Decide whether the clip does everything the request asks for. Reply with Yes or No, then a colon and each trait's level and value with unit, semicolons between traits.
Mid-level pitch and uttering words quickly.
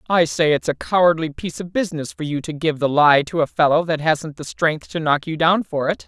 Yes: medium, 160 Hz; fast, 265 wpm